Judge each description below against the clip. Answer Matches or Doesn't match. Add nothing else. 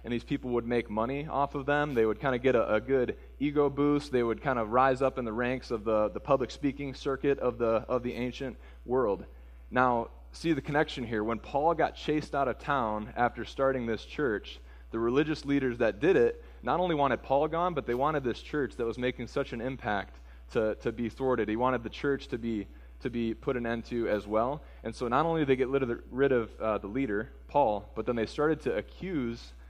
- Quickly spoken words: Matches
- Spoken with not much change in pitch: Doesn't match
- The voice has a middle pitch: Doesn't match